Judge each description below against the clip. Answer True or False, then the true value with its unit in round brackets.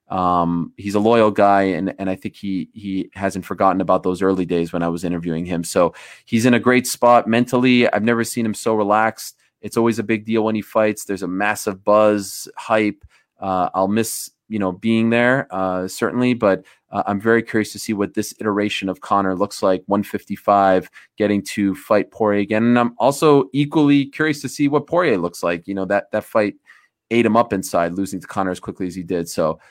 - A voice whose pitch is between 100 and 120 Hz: True (105 Hz)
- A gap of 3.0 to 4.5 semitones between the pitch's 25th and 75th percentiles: True (3.3 semitones)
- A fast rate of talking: True (215 wpm)